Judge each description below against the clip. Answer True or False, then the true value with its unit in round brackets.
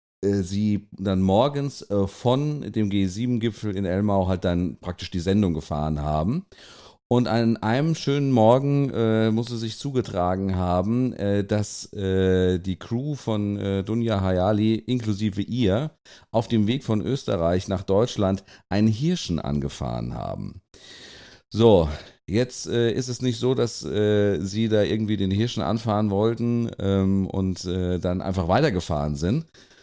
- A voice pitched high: False (105 Hz)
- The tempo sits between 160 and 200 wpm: False (145 wpm)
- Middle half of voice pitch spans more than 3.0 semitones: True (3.7 semitones)